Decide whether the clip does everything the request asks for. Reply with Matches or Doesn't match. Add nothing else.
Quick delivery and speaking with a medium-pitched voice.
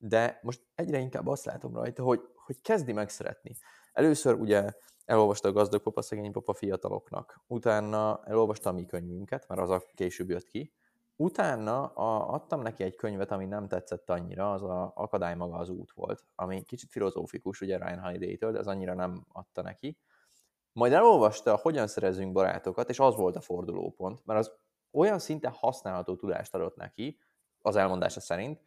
Doesn't match